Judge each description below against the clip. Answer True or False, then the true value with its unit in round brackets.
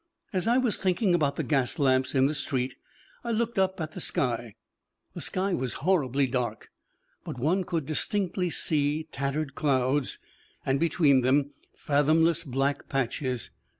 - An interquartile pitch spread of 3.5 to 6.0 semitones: True (4.7 semitones)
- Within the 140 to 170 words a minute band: True (150 wpm)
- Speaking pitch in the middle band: True (145 Hz)